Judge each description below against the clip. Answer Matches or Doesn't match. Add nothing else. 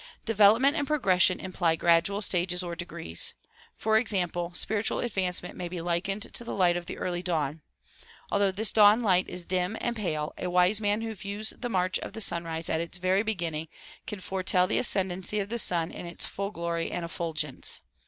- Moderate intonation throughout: Matches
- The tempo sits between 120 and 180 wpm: Doesn't match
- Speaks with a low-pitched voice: Doesn't match